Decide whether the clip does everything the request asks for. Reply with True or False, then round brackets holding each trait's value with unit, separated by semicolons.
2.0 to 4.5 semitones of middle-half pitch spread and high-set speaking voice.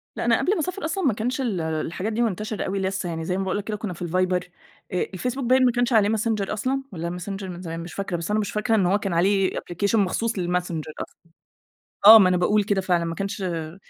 True (3.7 semitones; 195 Hz)